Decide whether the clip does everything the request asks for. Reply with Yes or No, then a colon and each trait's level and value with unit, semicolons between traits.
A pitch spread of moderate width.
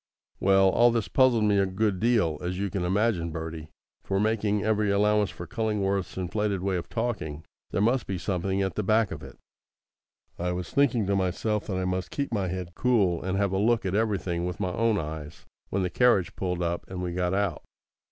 Yes: average, 3.0 semitones